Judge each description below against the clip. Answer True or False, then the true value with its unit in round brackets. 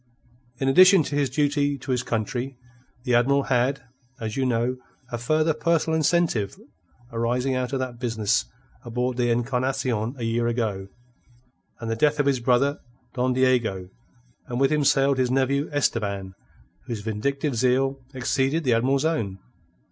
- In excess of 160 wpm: False (155 wpm)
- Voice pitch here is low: True (130 Hz)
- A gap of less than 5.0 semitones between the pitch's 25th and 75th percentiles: True (2.9 semitones)